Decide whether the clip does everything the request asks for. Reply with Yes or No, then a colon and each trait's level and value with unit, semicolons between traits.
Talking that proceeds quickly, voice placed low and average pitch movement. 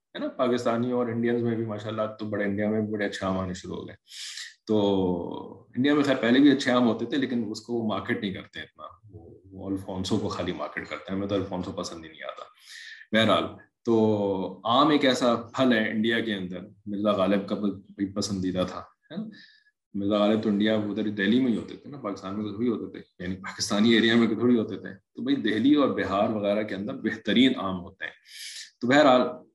Yes: fast, 215 wpm; low, 105 Hz; average, 3.2 semitones